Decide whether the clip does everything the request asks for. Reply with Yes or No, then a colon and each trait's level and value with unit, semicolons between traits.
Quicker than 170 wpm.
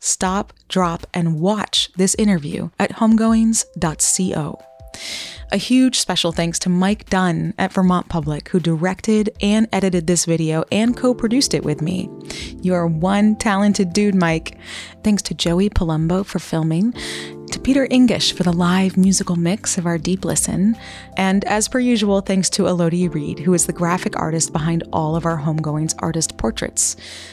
No: average, 160 wpm